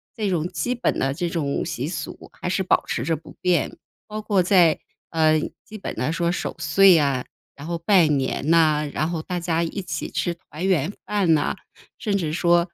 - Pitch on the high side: No, medium, 170 Hz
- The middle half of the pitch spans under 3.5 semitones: Yes, average, 3.0 semitones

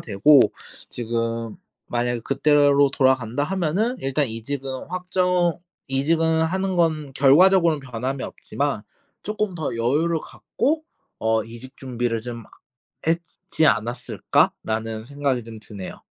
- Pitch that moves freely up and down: Yes, wide, 5.7 semitones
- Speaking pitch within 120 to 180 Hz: Yes, low, 135 Hz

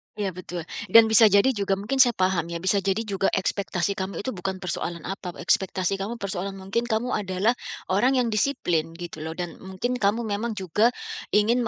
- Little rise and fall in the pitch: No, average, 3.2 semitones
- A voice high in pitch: Yes, high, 195 Hz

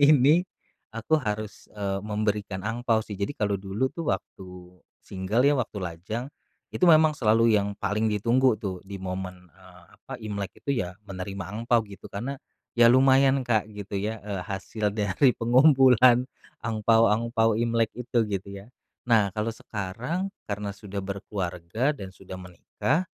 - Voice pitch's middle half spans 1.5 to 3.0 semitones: No, average, 3.7 semitones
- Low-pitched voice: Yes, low, 110 Hz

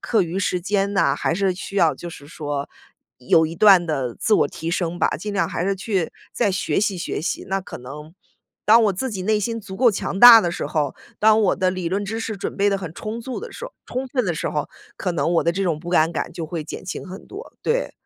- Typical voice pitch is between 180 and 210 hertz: Yes, high, 190 Hz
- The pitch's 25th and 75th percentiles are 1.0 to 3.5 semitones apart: No, average, 4.1 semitones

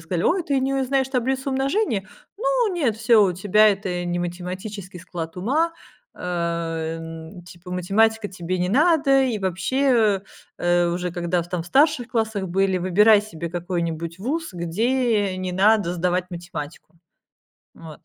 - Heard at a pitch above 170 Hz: Yes, high, 190 Hz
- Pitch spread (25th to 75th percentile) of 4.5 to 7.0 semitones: Yes, wide, 5.6 semitones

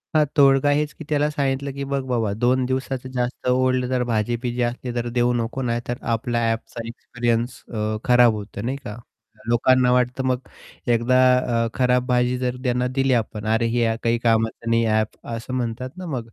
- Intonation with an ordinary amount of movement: No, narrow, 1.9 semitones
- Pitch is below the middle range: Yes, low, 125 Hz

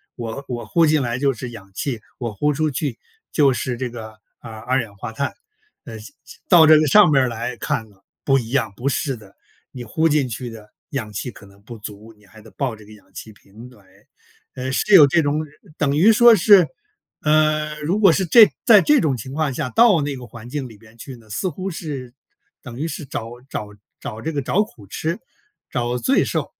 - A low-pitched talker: Yes, low, 130 Hz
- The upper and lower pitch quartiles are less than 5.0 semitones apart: No, average, 5.3 semitones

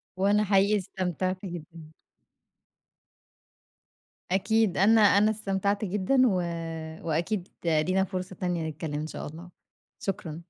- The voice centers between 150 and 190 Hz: Yes, medium, 185 Hz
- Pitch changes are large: No, average, 3.2 semitones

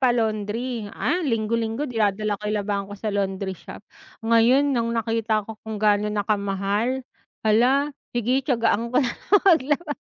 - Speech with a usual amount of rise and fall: Yes, average, 3.2 semitones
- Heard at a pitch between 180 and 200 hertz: No, high, 225 Hz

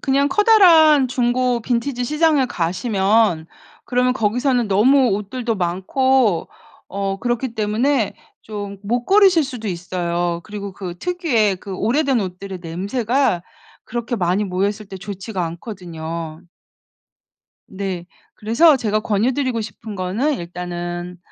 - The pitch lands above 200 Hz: Yes, high, 215 Hz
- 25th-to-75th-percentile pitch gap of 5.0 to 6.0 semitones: Yes, wide, 5.4 semitones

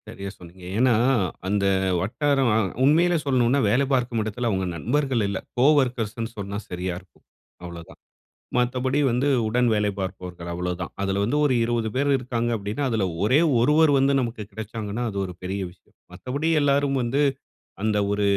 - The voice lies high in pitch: No, low, 115 Hz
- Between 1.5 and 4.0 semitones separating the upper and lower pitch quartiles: No, average, 4.9 semitones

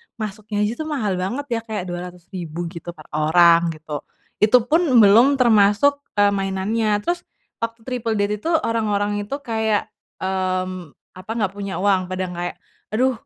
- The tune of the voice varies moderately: Yes, average, 3.4 semitones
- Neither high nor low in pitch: No, high, 205 Hz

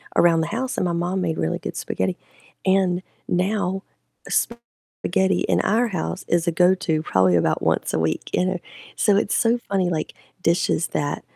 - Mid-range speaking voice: Yes, medium, 180 Hz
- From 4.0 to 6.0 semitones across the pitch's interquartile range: No, average, 3.1 semitones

